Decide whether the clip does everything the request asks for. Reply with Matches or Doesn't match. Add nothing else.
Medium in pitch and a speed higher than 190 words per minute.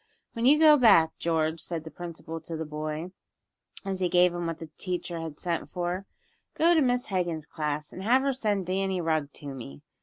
Matches